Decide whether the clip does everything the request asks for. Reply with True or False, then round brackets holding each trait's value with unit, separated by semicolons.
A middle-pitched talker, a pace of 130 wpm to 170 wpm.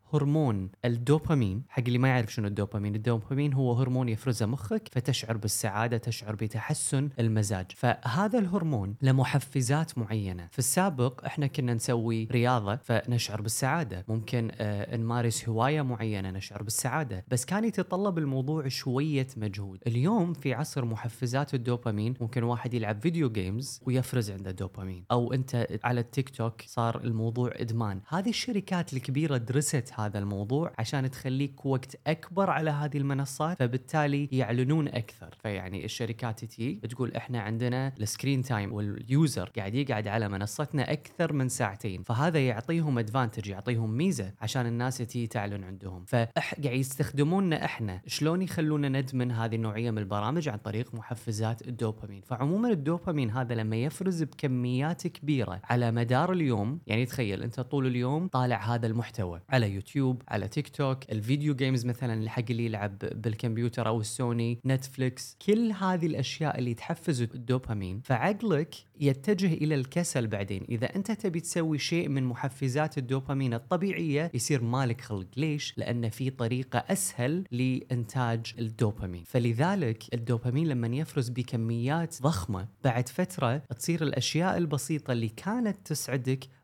False (125 Hz; 135 wpm)